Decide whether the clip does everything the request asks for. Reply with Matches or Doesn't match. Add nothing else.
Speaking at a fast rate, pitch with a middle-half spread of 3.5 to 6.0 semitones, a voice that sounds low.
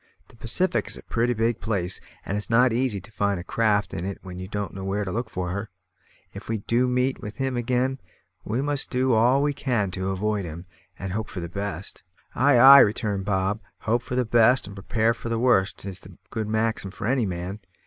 Matches